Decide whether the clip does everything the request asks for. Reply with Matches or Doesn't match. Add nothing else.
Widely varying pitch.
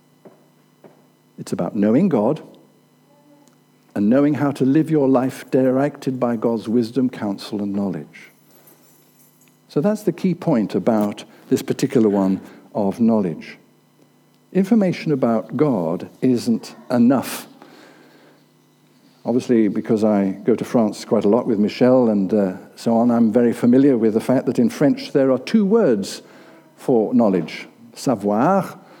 Doesn't match